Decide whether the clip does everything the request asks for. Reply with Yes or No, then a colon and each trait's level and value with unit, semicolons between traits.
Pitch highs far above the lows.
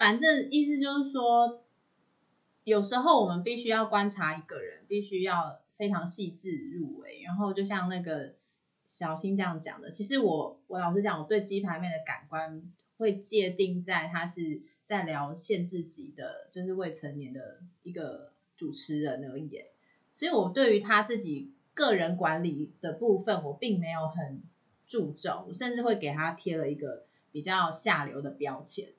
No: average, 5.0 semitones